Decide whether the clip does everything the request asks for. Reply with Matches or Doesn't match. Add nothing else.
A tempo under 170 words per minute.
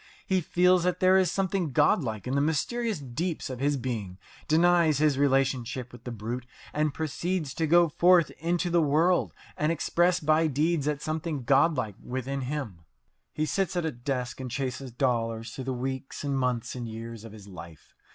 Doesn't match